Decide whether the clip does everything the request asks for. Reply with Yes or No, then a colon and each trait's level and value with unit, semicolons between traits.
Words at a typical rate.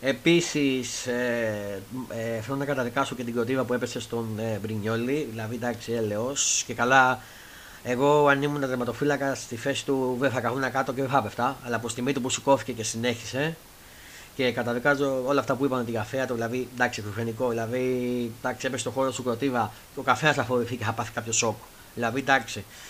No: fast, 190 wpm